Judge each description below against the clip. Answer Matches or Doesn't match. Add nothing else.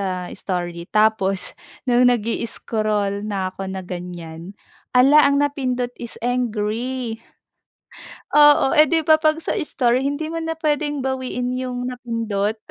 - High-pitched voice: Matches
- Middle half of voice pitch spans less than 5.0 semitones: Doesn't match